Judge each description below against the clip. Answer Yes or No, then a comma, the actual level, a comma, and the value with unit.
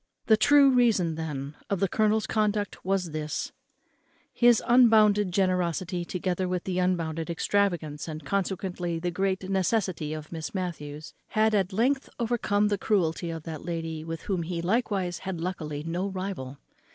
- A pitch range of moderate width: Yes, average, 3.8 semitones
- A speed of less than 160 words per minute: Yes, average, 150 wpm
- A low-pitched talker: No, medium, 185 Hz